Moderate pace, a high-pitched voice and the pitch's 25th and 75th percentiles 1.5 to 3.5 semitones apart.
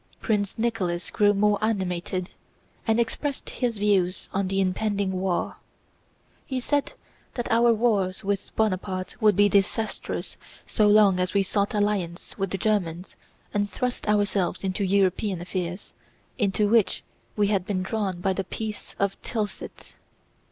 Yes: average, 145 wpm; high, 200 Hz; narrow, 2.4 semitones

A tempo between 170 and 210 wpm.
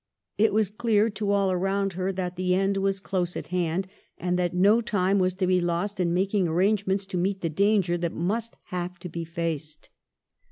Yes: average, 200 wpm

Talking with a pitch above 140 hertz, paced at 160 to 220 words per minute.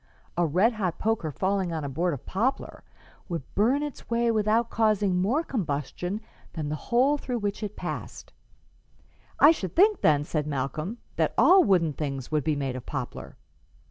Yes: high, 190 Hz; average, 175 wpm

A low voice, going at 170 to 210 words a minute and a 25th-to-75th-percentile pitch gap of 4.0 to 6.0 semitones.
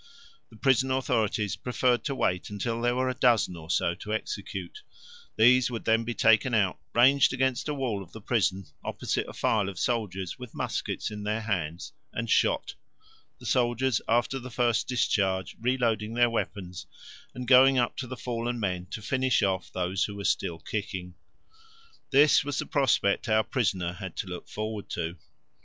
Yes: low, 115 Hz; average, 175 wpm; average, 4.4 semitones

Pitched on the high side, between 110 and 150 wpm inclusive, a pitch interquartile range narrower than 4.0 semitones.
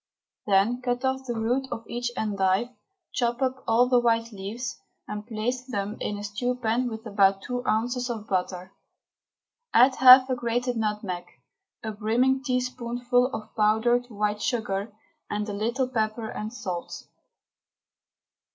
Yes: high, 230 Hz; average, 145 wpm; average, 2.9 semitones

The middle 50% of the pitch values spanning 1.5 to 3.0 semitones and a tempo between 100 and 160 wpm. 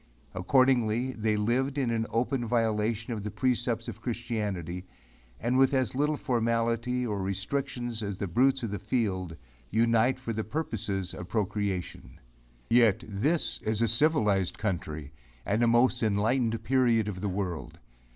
No: average, 3.4 semitones; average, 145 wpm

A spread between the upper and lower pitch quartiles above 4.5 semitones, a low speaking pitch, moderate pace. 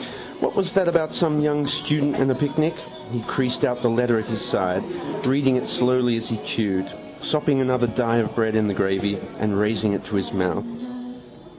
Yes: average, 5.0 semitones; low, 120 Hz; average, 195 wpm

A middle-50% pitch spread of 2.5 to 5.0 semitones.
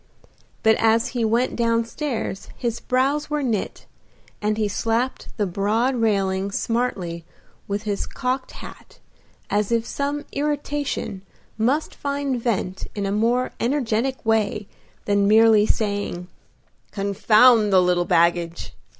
Yes: average, 3.8 semitones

